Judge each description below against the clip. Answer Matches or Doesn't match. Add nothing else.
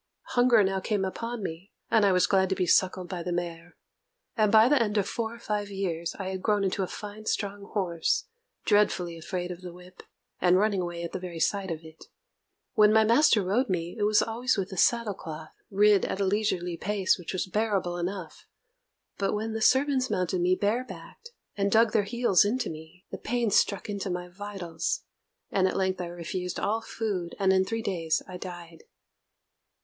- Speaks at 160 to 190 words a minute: Doesn't match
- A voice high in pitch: Matches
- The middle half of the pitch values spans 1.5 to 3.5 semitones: Matches